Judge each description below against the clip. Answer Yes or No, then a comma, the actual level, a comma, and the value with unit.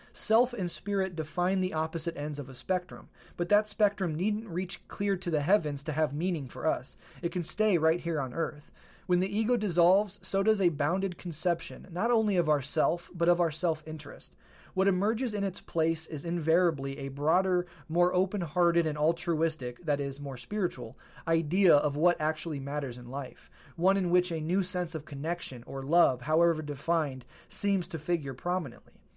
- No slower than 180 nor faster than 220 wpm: Yes, average, 185 wpm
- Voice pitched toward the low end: No, medium, 170 Hz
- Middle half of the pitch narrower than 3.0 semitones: No, average, 3.3 semitones